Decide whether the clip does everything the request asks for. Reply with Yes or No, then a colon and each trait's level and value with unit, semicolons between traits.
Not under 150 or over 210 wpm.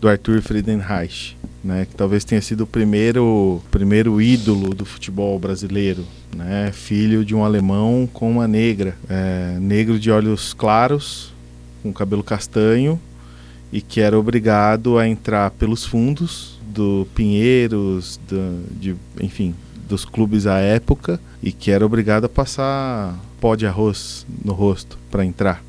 No: average, 140 wpm